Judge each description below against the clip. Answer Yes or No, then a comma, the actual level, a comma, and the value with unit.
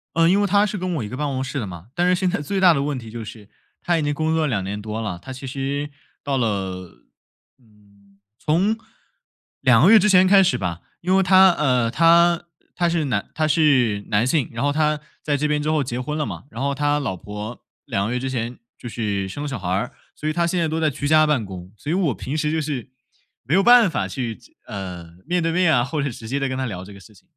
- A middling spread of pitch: No, wide, 6.4 semitones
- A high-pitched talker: No, medium, 140 Hz